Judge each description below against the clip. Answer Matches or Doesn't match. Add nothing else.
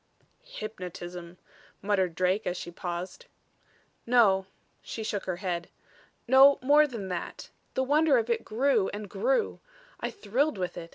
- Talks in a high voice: Matches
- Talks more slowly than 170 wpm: Matches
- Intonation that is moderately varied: Doesn't match